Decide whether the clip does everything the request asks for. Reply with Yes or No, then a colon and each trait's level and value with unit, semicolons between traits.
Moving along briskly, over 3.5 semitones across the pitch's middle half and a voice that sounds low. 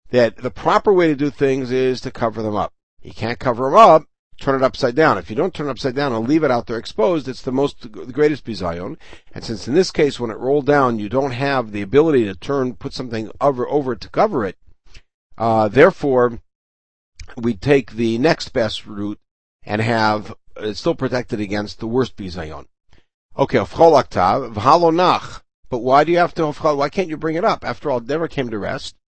Yes: fast, 210 wpm; average, 4.7 semitones; low, 125 Hz